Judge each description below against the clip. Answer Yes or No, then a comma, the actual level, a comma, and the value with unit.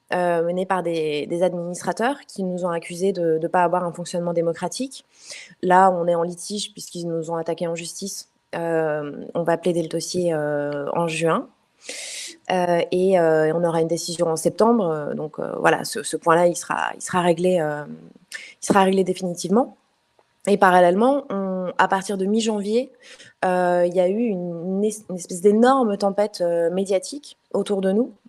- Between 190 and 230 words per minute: No, average, 180 wpm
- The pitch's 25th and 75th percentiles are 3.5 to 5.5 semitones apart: No, average, 2.8 semitones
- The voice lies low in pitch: No, medium, 180 Hz